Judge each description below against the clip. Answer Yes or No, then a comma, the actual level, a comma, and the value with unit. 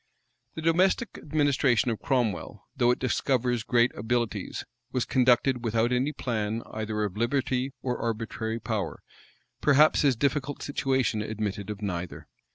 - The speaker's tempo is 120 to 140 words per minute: Yes, slow, 135 wpm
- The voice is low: Yes, low, 120 Hz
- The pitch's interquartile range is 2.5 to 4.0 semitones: Yes, average, 3.5 semitones